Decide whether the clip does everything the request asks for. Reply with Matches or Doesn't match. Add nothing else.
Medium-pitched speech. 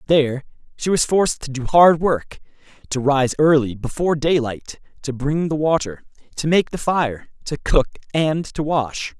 Matches